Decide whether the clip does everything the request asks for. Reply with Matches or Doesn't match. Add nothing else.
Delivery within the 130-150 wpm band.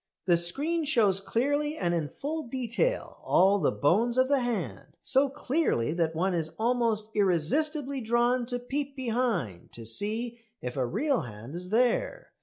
Doesn't match